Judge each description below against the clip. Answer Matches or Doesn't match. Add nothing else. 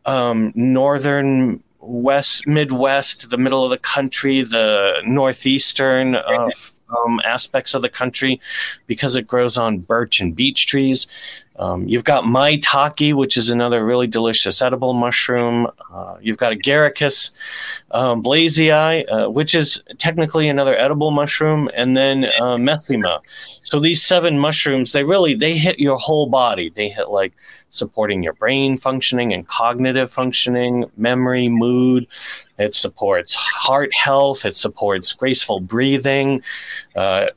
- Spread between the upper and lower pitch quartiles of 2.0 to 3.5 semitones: Matches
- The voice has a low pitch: Matches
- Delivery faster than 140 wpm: Doesn't match